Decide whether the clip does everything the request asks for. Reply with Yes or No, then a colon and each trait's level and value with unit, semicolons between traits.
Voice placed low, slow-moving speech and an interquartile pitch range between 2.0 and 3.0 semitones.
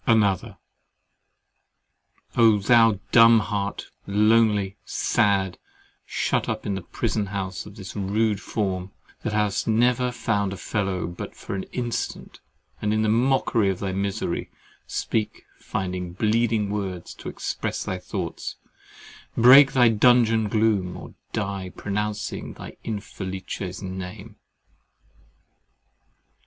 Yes: low, 105 Hz; slow, 120 wpm; average, 2.7 semitones